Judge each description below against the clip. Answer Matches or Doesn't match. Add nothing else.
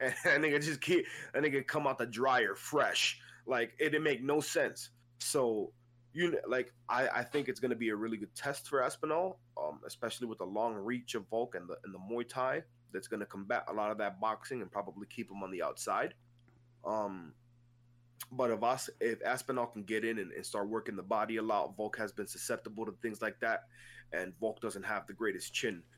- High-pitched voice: Doesn't match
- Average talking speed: Doesn't match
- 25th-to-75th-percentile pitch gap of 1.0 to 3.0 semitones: Matches